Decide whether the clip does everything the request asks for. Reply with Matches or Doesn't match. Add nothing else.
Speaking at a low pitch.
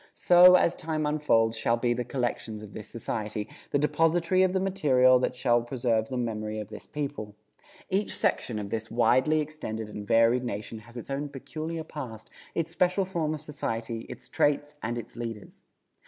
Matches